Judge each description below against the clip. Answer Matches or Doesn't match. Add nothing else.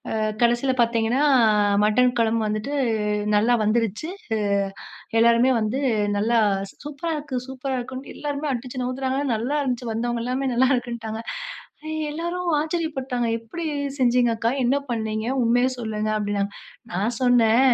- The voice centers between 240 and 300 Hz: Matches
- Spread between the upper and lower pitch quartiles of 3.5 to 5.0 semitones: Doesn't match